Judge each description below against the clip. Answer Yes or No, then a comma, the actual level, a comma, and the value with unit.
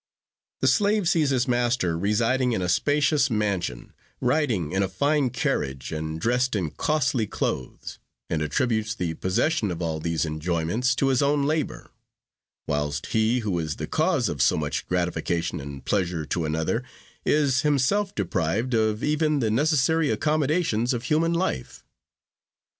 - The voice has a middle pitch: No, low, 115 Hz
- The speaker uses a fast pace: No, average, 150 wpm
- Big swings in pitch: Yes, wide, 9.0 semitones